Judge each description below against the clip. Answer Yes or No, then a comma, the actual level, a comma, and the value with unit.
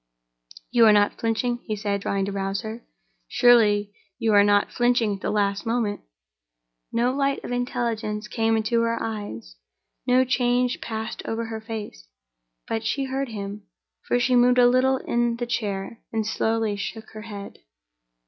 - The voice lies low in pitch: No, high, 225 Hz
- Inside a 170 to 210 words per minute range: No, average, 160 wpm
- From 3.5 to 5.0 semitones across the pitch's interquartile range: No, average, 2.8 semitones